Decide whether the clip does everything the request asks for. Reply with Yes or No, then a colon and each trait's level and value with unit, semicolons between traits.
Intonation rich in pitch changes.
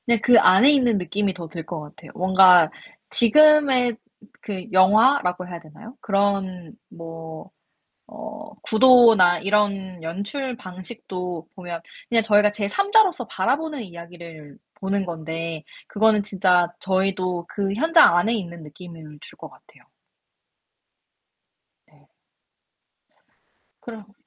No: average, 4.4 semitones